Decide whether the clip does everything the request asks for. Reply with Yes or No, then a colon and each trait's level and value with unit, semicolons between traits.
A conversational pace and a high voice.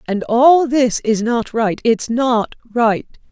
Yes: average, 165 wpm; high, 235 Hz